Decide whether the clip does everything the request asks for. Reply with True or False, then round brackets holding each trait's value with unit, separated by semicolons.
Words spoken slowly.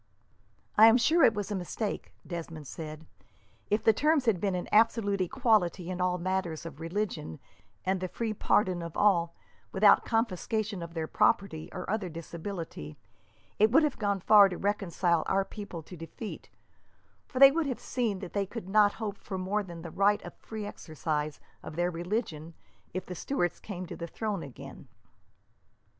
False (175 wpm)